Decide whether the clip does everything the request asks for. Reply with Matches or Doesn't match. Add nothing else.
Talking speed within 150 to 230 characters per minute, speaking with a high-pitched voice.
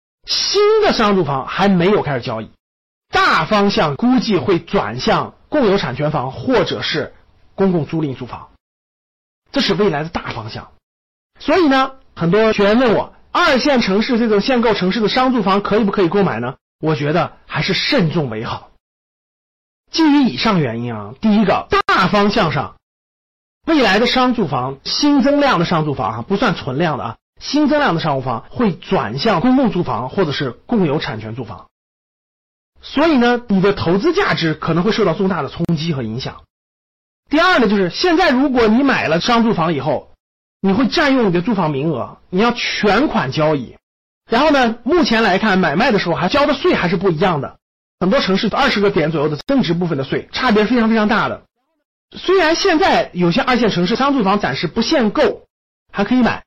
Doesn't match